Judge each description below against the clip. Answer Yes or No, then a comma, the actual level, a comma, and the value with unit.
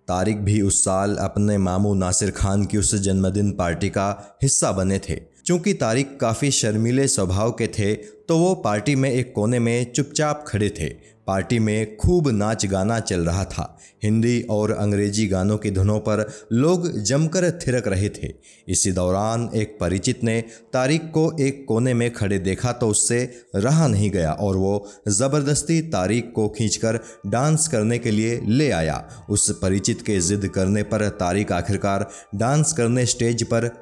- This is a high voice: No, low, 105 Hz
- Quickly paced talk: No, average, 165 wpm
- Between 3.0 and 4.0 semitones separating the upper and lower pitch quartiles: Yes, average, 3.5 semitones